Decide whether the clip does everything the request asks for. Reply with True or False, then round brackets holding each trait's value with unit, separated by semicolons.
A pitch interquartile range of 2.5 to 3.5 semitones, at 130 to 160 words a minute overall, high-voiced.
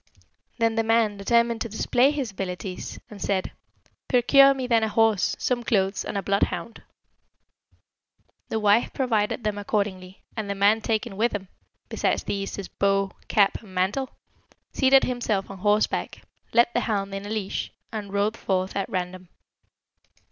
True (2.8 semitones; 155 wpm; 210 Hz)